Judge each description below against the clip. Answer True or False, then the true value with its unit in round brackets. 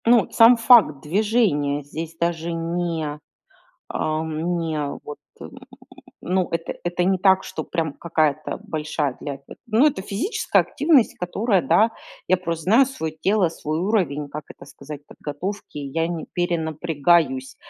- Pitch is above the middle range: False (165 Hz)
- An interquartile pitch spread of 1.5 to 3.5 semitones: False (4.1 semitones)